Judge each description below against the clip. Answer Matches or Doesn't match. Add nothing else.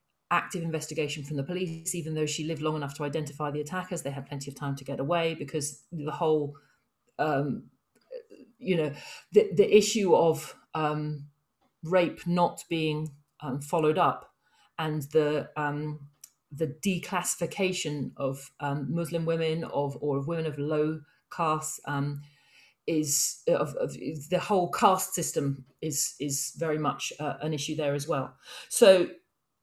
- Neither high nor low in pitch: Matches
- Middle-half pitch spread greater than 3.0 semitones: Doesn't match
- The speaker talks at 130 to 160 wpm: Matches